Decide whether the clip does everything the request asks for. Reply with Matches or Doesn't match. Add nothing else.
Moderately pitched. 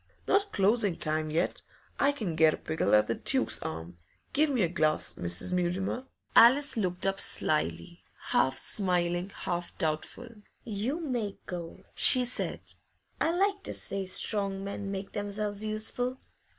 Doesn't match